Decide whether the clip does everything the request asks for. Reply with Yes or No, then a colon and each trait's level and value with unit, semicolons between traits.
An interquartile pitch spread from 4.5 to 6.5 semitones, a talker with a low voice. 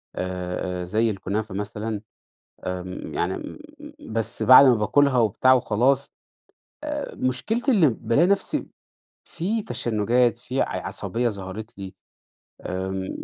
Yes: average, 5.1 semitones; low, 115 Hz